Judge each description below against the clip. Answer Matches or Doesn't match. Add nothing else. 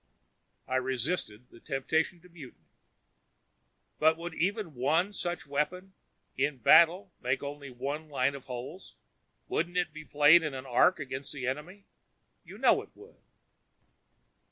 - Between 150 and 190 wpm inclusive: Doesn't match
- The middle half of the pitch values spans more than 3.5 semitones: Matches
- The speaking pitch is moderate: Matches